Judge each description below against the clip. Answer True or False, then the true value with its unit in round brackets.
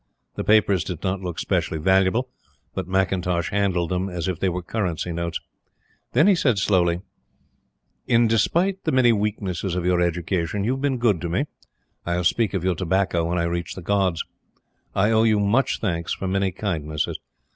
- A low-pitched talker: True (95 Hz)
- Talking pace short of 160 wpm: False (185 wpm)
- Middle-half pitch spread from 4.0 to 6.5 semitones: False (3.4 semitones)